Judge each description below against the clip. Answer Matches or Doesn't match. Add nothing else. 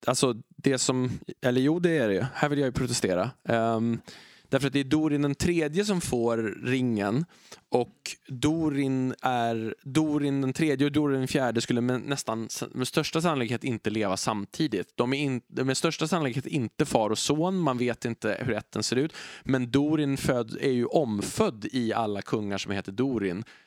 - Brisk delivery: Doesn't match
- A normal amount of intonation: Matches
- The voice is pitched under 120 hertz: Doesn't match